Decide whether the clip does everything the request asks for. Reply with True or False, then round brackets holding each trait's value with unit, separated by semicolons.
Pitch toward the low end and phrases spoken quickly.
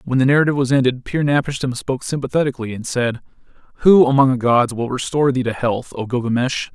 True (130 Hz; 215 wpm)